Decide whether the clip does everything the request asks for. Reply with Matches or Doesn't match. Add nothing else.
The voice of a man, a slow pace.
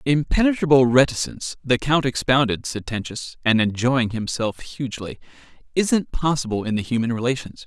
Matches